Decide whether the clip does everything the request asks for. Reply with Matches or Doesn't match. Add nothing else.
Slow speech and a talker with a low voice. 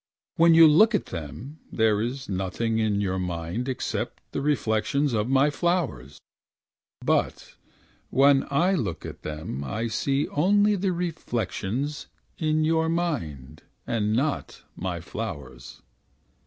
Matches